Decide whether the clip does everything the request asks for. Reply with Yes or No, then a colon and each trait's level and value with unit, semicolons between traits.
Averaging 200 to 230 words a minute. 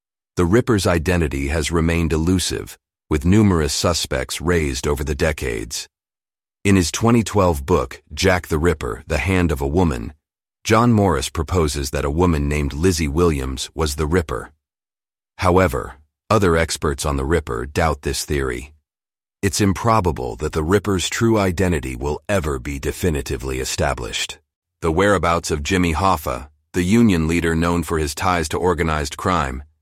No: average, 145 wpm